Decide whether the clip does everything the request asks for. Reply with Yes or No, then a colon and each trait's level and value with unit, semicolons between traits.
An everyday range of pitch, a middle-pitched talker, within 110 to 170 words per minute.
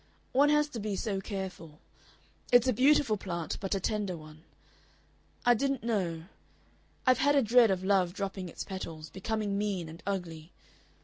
No: average, 4.9 semitones; high, 200 Hz; average, 160 wpm